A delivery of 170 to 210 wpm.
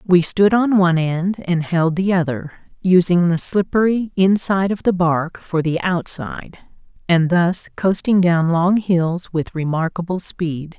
No: average, 155 wpm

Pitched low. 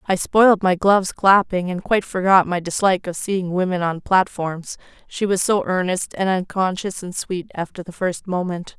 No: medium, 185 Hz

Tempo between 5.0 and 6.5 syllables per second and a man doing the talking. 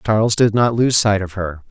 Yes: 5.2 syllables/s; male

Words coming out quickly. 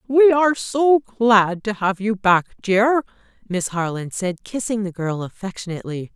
No: average, 155 wpm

